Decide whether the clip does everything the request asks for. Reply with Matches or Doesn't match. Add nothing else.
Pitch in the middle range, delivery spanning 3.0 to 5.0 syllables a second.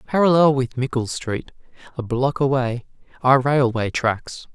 Doesn't match